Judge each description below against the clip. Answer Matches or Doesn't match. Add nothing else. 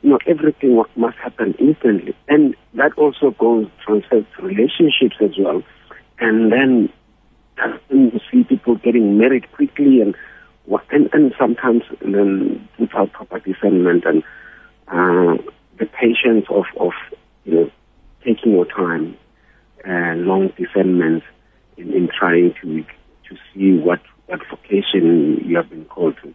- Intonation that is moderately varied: Doesn't match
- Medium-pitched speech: Doesn't match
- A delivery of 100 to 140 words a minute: Matches